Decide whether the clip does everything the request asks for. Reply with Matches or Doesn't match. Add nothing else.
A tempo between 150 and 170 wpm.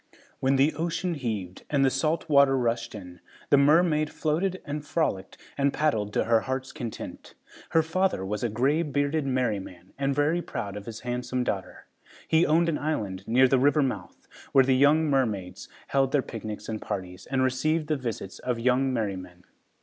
Doesn't match